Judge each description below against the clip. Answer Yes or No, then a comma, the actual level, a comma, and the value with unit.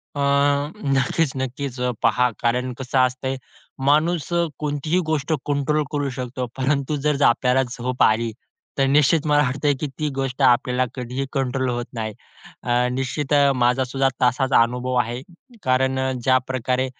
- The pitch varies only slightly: Yes, narrow, 2.3 semitones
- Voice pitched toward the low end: Yes, low, 130 Hz